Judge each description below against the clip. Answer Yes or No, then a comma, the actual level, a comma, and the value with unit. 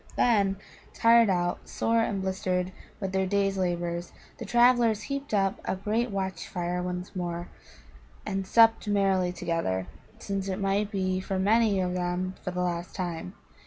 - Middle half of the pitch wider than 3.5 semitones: No, narrow, 2.5 semitones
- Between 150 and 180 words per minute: Yes, average, 160 wpm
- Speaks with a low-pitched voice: No, high, 190 Hz